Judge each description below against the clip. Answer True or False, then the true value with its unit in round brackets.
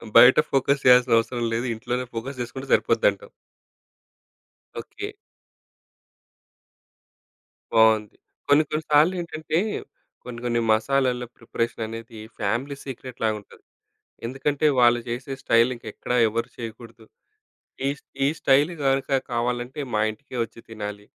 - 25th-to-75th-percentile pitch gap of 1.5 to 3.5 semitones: True (3.0 semitones)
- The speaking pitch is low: True (120 Hz)